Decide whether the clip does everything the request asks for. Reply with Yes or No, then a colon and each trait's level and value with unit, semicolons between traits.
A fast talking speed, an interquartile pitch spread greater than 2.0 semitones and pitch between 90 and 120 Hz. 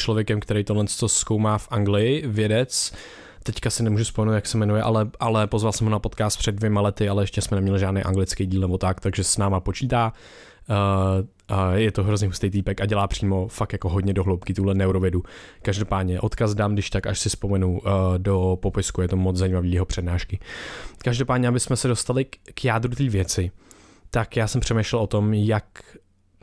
Yes: fast, 200 wpm; narrow, 2.4 semitones; low, 100 Hz